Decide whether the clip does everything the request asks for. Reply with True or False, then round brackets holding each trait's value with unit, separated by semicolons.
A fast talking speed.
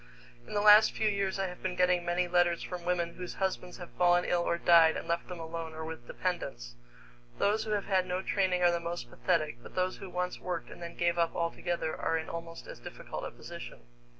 True (230 wpm)